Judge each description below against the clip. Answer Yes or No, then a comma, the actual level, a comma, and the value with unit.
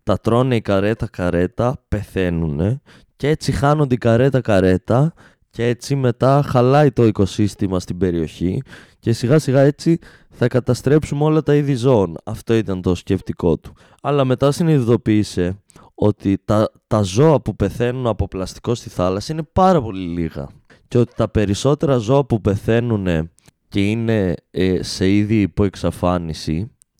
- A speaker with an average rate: Yes, average, 145 wpm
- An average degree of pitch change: No, wide, 5.7 semitones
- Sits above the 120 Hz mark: No, low, 110 Hz